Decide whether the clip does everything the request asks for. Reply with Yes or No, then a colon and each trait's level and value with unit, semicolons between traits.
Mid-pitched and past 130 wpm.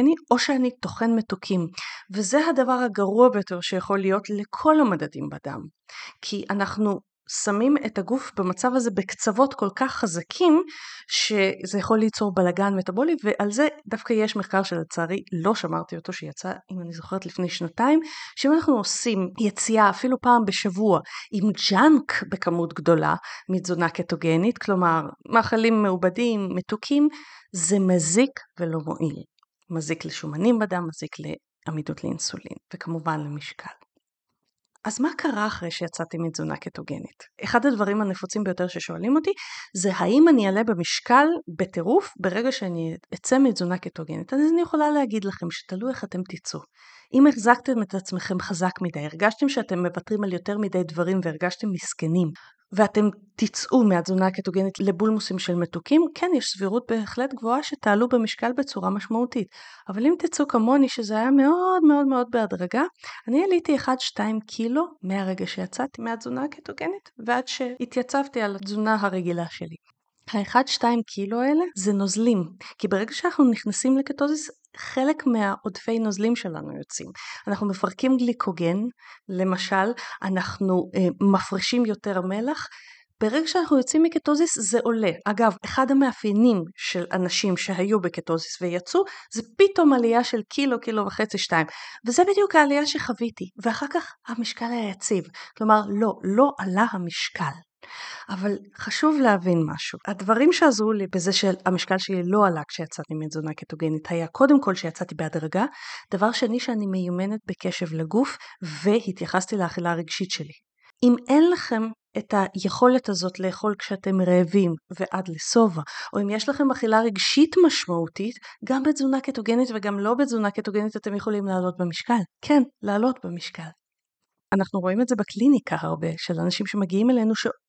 No: high, 210 Hz; average, 140 wpm